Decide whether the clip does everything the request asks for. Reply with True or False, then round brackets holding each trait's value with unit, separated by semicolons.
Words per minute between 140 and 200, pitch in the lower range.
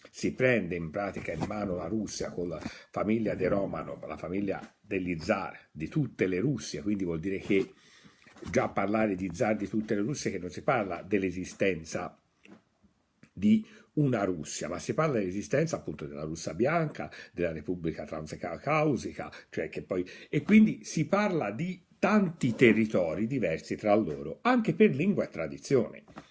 True (160 wpm; 105 Hz)